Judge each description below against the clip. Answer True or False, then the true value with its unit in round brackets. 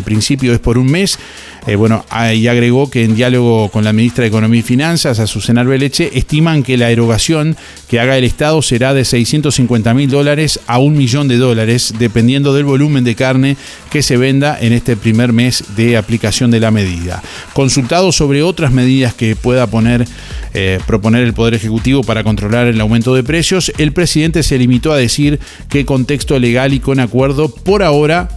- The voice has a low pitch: True (125 Hz)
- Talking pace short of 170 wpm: False (185 wpm)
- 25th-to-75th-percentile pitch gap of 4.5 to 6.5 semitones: False (3.4 semitones)